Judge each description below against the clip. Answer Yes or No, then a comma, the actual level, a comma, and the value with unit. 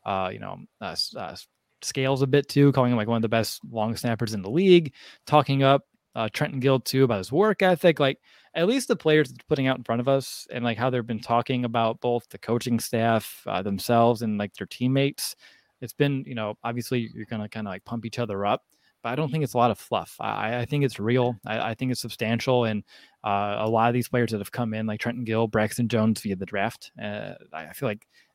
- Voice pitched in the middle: No, low, 120 Hz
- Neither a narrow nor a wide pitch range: Yes, average, 3.3 semitones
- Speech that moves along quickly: Yes, fast, 245 wpm